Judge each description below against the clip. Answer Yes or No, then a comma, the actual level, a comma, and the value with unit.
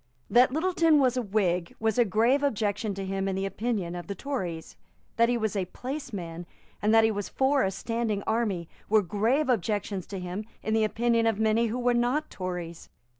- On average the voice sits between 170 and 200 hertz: No, high, 220 Hz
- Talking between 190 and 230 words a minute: Yes, average, 200 wpm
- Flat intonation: No, average, 3.9 semitones